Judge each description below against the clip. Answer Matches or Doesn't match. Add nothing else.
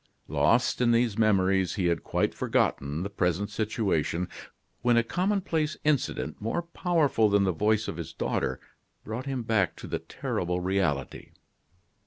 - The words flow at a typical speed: Matches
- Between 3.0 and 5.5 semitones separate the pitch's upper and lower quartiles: Matches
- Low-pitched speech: Matches